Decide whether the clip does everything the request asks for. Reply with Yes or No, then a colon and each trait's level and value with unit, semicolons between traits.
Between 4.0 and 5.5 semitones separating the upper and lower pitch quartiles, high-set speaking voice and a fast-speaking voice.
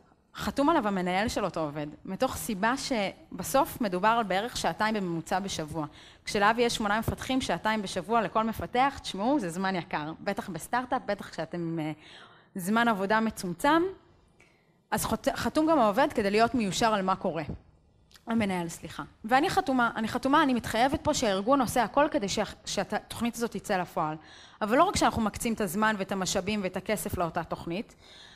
Yes: average, 4.7 semitones; high, 210 Hz; fast, 160 wpm